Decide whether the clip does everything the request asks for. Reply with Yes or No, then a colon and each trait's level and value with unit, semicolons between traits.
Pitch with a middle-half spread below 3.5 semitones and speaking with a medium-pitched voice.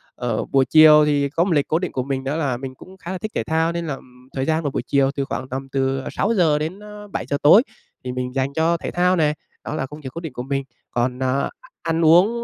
No: average, 4.0 semitones; medium, 150 Hz